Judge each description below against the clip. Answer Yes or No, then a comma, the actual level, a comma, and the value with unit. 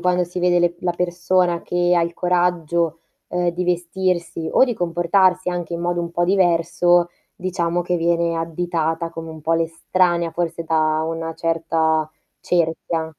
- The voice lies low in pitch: No, medium, 170 Hz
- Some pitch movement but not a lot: No, narrow, 1.2 semitones